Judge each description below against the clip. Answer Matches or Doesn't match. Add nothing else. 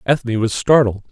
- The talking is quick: Doesn't match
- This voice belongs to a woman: Doesn't match